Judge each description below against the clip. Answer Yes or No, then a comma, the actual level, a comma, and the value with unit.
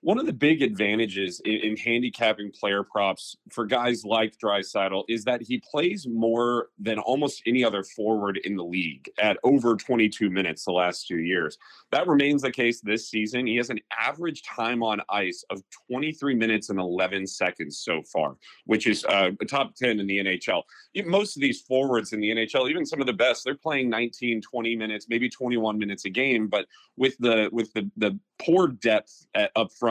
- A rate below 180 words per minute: No, average, 195 wpm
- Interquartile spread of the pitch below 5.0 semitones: Yes, average, 3.1 semitones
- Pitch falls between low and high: No, low, 110 Hz